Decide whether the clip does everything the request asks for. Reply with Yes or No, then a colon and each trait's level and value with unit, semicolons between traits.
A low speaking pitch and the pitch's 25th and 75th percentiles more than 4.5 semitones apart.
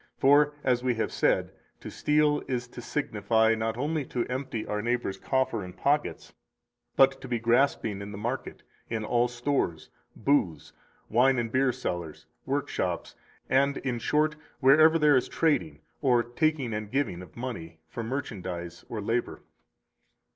No: low, 120 Hz; average, 4.0 semitones